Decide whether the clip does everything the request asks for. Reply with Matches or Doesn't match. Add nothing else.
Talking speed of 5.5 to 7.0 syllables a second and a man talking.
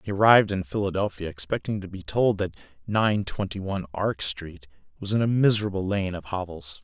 Matches